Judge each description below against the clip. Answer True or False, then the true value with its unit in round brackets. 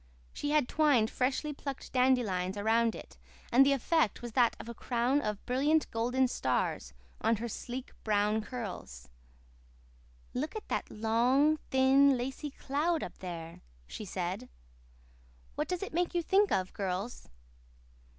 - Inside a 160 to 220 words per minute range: False (145 wpm)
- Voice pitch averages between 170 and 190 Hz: False (245 Hz)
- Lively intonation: False (4.8 semitones)